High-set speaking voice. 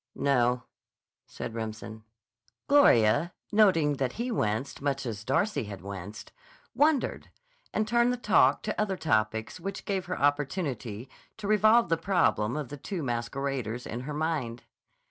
No: medium, 140 Hz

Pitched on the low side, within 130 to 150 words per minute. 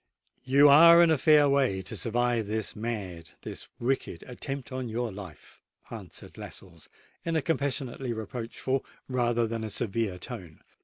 Yes: low, 120 Hz; average, 145 wpm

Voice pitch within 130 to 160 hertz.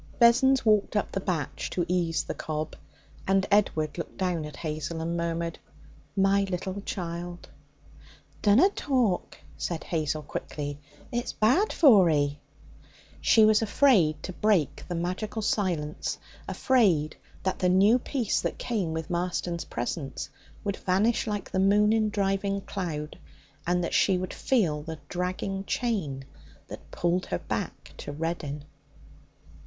No: medium, 185 Hz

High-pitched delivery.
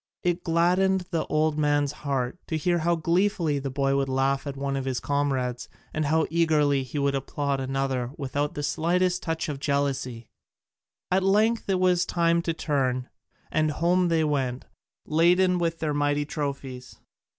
No: medium, 150 Hz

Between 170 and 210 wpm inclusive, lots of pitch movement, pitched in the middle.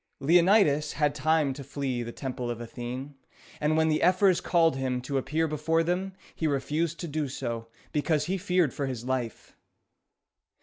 No: average, 175 wpm; average, 3.9 semitones; medium, 150 Hz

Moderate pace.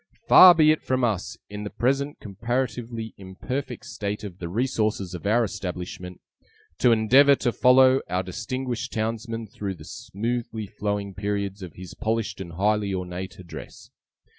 Yes: average, 150 wpm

